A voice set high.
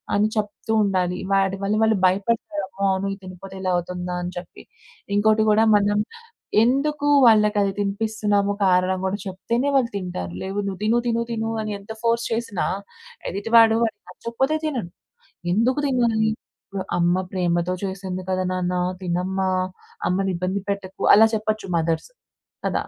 Yes: high, 200 Hz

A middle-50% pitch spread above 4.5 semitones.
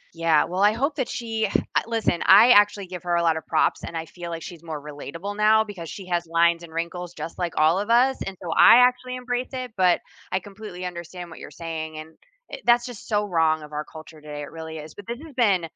Yes: average, 4.9 semitones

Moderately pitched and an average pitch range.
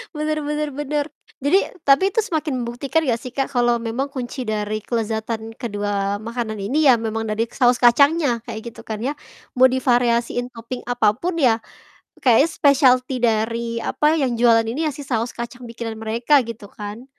No: high, 240 Hz; average, 3.3 semitones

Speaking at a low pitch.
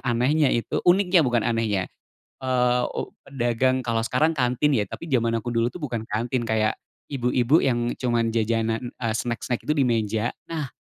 Yes: low, 120 Hz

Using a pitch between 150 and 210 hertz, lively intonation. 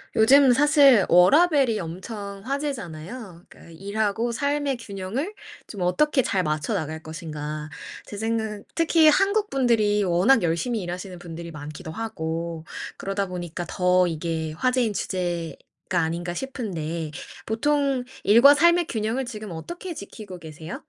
Yes: high, 200 Hz; wide, 7.2 semitones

